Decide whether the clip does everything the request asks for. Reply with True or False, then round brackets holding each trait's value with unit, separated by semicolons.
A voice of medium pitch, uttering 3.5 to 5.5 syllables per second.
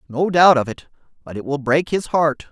True (150 Hz; 5.0 syllables/s)